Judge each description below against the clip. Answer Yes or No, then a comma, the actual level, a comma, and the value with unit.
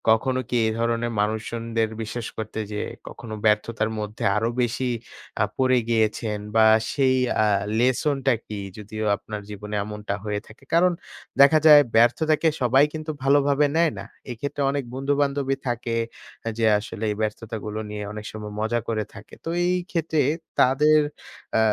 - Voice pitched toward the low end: Yes, low, 115 Hz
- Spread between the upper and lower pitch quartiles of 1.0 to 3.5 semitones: No, average, 4.3 semitones